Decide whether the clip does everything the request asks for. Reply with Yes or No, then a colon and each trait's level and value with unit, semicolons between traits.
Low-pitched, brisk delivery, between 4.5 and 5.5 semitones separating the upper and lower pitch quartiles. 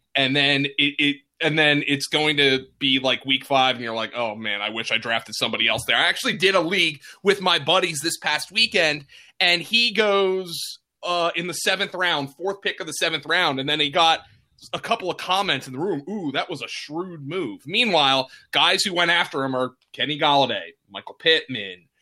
No: medium, 155 Hz; fast, 215 wpm; average, 5.2 semitones